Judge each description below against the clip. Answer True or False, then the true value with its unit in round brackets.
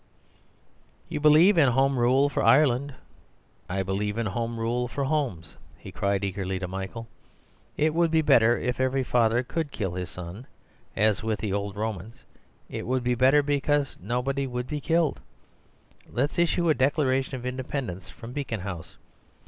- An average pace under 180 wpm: True (165 wpm)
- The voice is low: True (125 Hz)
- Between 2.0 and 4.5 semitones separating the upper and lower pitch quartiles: False (5.3 semitones)